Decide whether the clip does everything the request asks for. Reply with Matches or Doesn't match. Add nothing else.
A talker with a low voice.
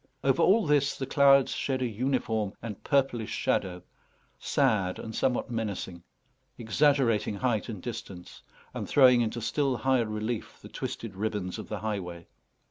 Matches